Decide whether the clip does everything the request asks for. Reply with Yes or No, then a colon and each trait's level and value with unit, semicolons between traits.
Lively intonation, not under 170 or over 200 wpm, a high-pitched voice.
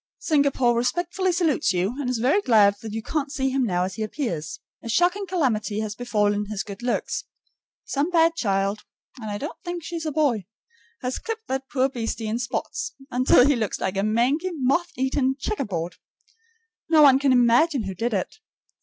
Yes: wide, 6.0 semitones; average, 185 wpm; very high, 255 Hz